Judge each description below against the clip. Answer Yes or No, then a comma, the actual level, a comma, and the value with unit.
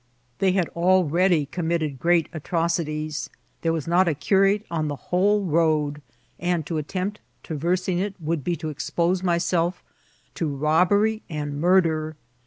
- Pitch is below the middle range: No, medium, 170 Hz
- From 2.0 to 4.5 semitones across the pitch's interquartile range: Yes, average, 2.9 semitones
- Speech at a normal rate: Yes, average, 150 wpm